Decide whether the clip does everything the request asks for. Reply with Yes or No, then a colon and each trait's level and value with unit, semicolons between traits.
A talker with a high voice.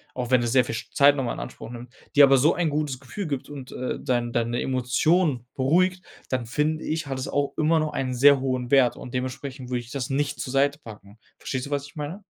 No: low, 135 Hz